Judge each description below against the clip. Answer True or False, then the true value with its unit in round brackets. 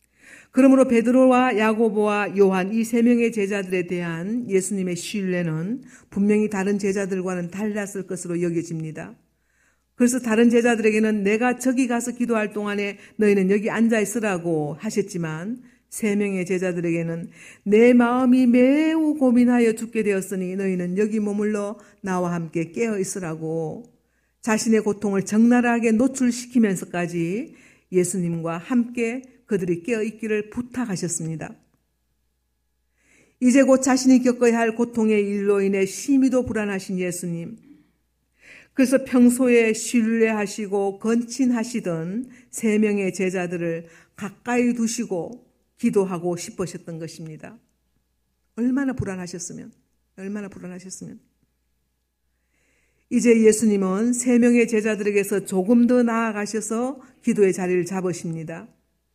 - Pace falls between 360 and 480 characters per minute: False (295 characters per minute)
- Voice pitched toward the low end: False (210 Hz)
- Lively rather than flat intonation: False (4.5 semitones)